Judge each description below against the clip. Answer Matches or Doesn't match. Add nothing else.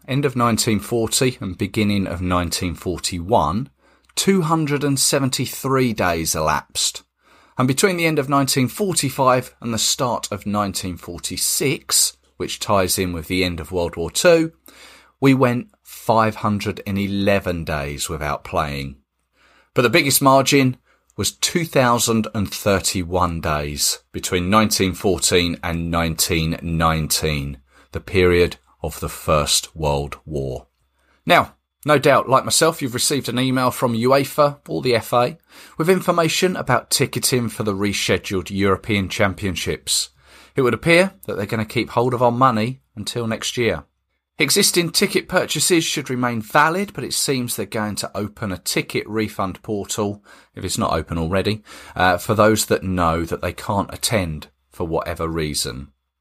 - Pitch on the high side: Doesn't match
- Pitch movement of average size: Doesn't match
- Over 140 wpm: Doesn't match